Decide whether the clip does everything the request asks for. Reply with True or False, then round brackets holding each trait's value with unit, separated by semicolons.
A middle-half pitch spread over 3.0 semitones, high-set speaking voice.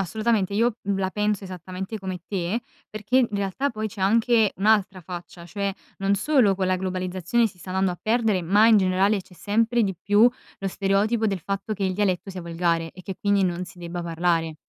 False (2.7 semitones; 195 Hz)